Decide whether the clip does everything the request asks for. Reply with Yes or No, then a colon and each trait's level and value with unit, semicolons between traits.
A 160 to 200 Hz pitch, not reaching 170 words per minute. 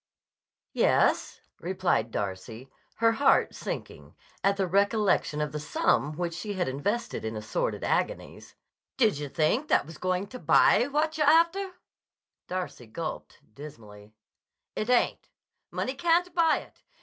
Yes: high, 190 Hz; average, 140 wpm